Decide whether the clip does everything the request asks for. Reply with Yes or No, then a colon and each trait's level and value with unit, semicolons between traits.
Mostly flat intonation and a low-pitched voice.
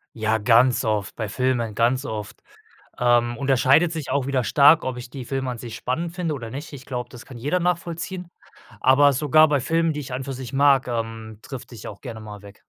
No: average, 3.8 semitones; low, 130 Hz